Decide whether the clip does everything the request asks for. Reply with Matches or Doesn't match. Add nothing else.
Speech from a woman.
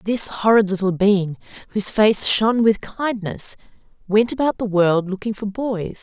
Matches